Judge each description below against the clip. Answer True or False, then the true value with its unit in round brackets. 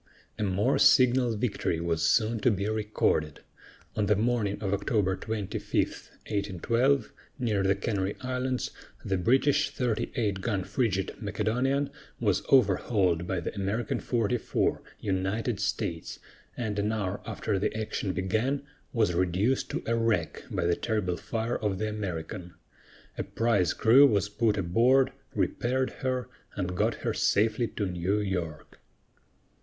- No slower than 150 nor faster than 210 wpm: False (140 wpm)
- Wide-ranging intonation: False (3.8 semitones)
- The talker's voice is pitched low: True (105 Hz)